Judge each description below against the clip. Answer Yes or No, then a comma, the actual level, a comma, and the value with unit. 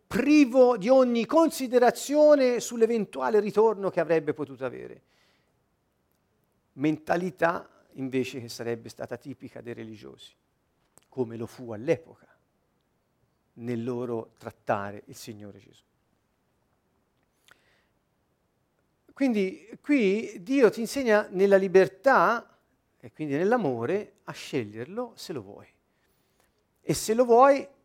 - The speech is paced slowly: Yes, slow, 100 wpm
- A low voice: No, high, 190 Hz